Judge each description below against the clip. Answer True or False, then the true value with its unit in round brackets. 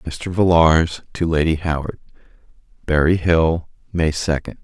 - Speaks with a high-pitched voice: False (80 Hz)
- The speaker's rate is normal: False (115 wpm)